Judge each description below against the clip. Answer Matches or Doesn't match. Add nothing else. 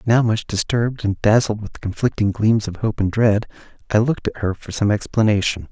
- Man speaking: Matches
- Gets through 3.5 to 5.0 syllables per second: Doesn't match